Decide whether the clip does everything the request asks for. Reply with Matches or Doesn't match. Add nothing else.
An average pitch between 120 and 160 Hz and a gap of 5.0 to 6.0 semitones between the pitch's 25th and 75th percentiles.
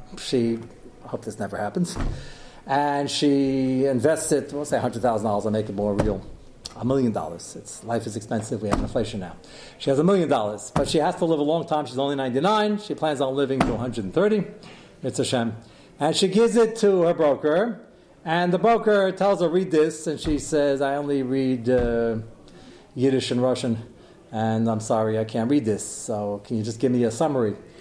Matches